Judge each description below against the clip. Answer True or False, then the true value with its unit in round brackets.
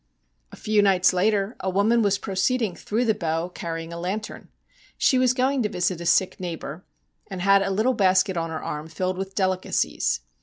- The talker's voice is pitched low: False (190 Hz)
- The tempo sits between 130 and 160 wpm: False (195 wpm)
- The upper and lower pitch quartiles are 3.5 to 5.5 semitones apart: False (3.1 semitones)